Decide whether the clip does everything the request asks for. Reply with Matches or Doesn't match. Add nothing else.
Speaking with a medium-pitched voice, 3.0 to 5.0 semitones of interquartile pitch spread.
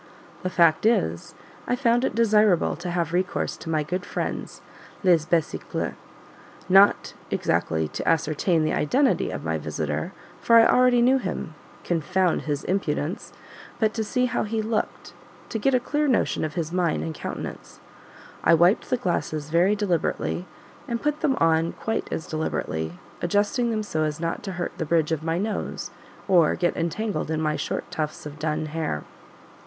Doesn't match